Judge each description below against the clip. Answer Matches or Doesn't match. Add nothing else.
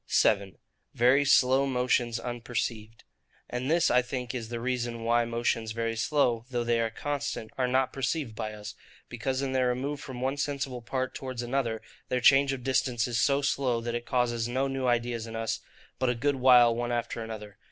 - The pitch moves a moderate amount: Doesn't match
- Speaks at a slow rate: Doesn't match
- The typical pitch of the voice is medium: Doesn't match